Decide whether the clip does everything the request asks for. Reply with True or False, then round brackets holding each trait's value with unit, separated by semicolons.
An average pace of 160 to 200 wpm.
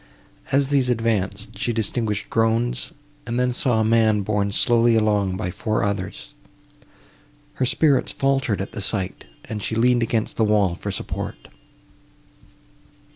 False (140 wpm)